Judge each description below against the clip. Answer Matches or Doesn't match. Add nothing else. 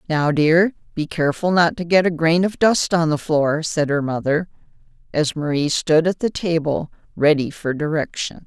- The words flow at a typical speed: Matches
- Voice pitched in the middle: Matches